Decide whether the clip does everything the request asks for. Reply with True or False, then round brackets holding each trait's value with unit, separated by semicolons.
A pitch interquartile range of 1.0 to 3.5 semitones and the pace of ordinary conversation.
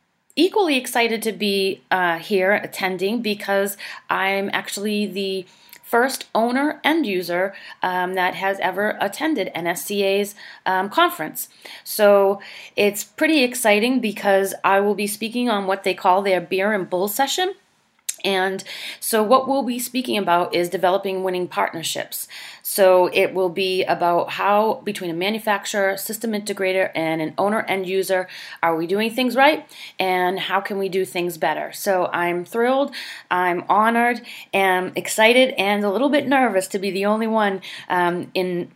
True (3.0 semitones; 155 wpm)